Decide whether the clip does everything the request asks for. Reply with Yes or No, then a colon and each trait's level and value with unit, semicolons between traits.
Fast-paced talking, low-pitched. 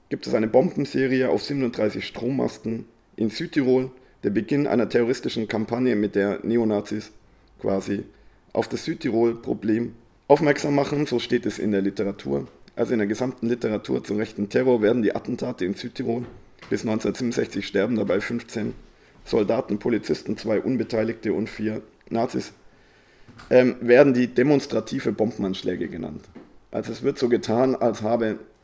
No: average, 140 wpm; low, 115 Hz